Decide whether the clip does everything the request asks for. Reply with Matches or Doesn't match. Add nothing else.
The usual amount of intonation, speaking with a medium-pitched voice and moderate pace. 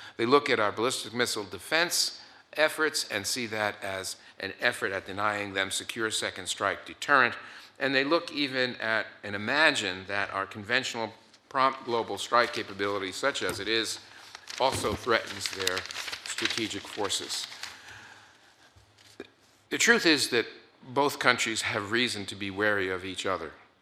Doesn't match